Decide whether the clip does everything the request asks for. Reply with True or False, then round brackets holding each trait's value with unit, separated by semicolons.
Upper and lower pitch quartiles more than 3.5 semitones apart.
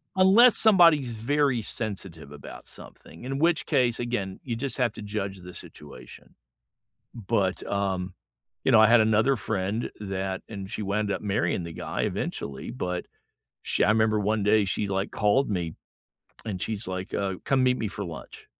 True (4.1 semitones)